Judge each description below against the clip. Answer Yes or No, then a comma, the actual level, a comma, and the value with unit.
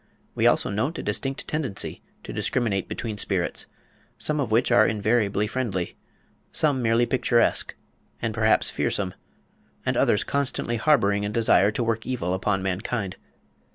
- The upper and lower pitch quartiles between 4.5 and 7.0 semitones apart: No, average, 3.6 semitones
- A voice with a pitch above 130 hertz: No, low, 110 Hz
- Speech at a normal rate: Yes, average, 145 wpm